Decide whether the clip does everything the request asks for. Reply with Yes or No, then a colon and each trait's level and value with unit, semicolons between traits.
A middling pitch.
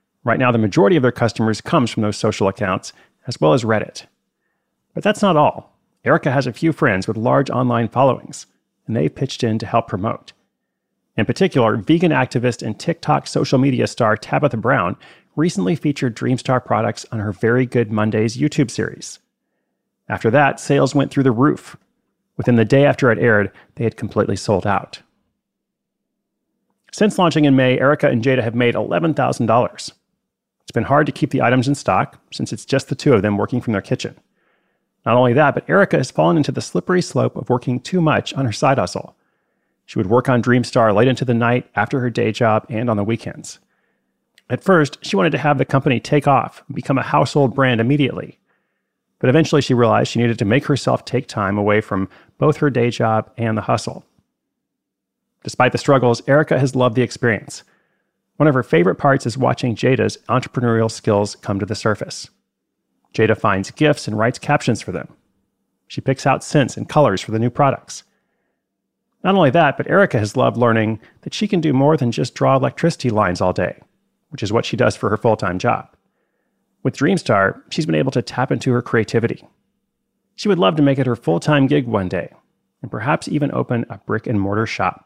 No: low, 125 Hz